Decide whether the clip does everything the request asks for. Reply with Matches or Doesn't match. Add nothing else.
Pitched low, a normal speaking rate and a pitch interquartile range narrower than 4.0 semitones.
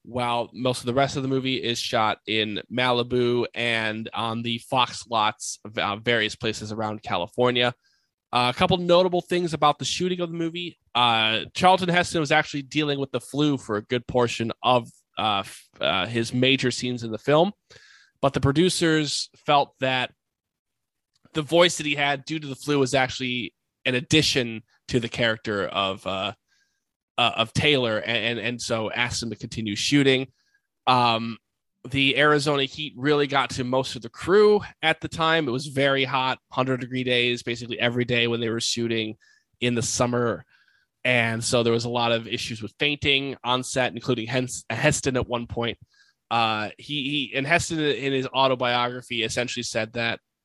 Matches